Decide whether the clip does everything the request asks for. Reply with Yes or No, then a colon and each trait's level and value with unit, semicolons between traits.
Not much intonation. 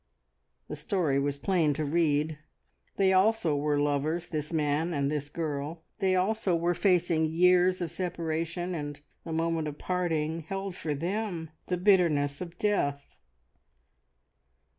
No: average, 3.4 semitones